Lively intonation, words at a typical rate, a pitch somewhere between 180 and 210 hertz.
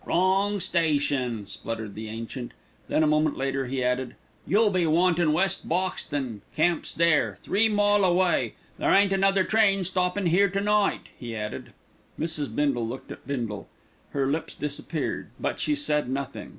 No: wide, 6.2 semitones; average, 160 wpm; medium, 160 Hz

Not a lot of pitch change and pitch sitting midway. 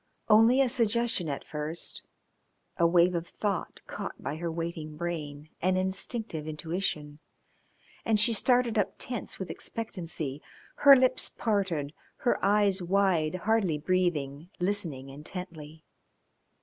No: average, 5.0 semitones; medium, 180 Hz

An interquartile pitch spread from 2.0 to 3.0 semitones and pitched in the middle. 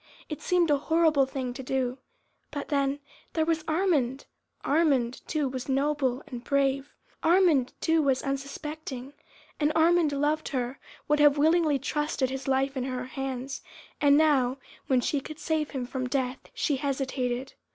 No: narrow, 2.6 semitones; very high, 280 Hz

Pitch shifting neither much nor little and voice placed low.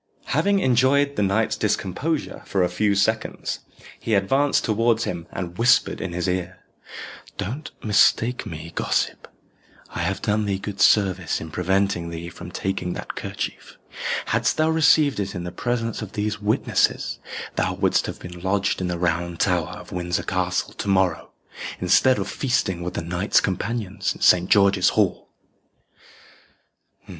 Yes: average, 4.1 semitones; low, 100 Hz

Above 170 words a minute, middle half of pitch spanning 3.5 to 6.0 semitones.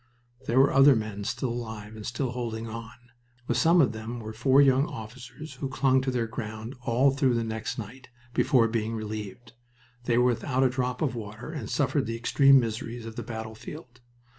No: average, 190 wpm; average, 2.9 semitones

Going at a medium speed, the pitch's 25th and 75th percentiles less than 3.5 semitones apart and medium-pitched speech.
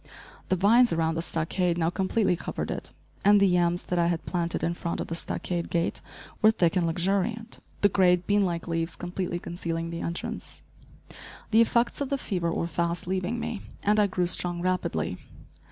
Yes: average, 185 wpm; average, 2.8 semitones; medium, 180 Hz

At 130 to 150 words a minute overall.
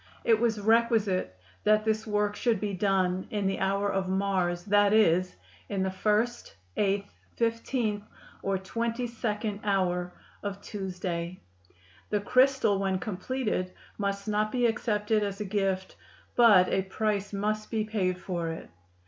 Yes: average, 145 wpm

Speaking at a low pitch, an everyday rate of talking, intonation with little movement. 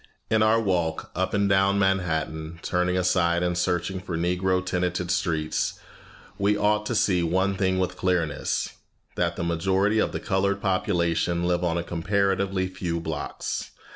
Yes: very low, 90 Hz; average, 155 wpm; narrow, 2.2 semitones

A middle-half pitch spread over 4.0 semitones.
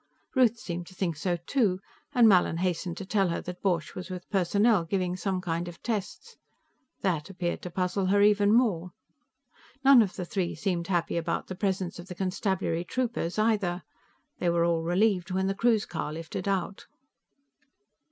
No: average, 2.7 semitones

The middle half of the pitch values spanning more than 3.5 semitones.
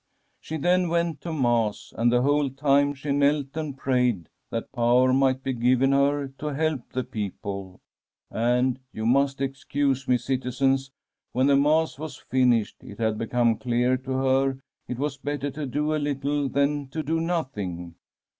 No: average, 2.7 semitones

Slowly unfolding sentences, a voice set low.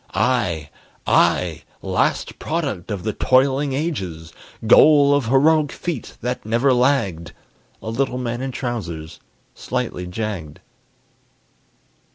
Yes: slow, 110 wpm; low, 120 Hz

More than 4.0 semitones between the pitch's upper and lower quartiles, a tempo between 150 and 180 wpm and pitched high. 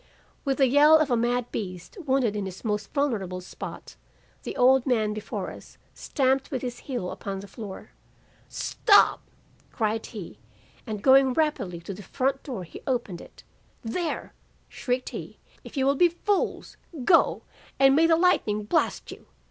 Yes: average, 4.9 semitones; average, 165 wpm; high, 245 Hz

